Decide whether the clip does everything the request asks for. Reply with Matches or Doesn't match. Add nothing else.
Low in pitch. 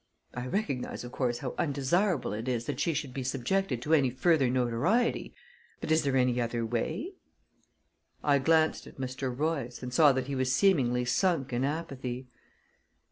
Matches